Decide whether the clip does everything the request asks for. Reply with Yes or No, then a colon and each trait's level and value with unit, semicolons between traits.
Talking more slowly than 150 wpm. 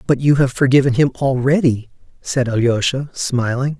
Yes: average, 140 wpm